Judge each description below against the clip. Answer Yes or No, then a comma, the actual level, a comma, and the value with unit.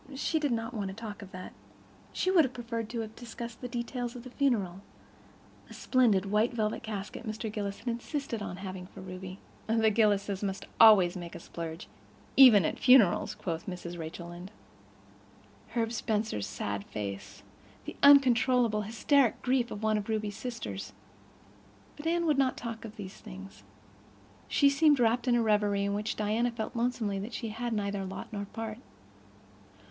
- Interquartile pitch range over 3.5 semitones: Yes, average, 4.2 semitones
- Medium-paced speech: Yes, average, 165 wpm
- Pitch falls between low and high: No, high, 215 Hz